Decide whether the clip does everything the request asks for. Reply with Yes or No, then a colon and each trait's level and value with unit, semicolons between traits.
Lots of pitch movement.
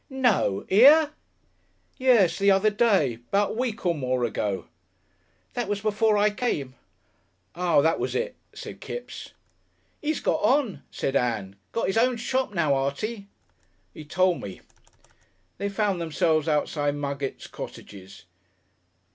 Yes: wide, 8.1 semitones